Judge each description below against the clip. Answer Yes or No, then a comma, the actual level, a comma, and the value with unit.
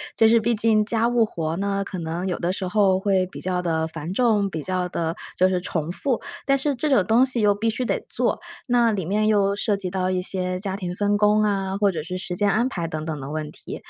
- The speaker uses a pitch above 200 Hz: No, high, 195 Hz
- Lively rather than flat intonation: No, average, 3.2 semitones